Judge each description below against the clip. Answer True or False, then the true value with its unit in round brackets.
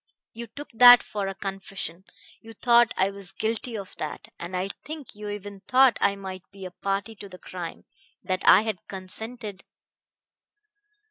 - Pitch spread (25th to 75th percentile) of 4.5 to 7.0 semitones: False (3.0 semitones)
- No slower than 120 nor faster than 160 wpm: False (170 wpm)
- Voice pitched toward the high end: True (200 Hz)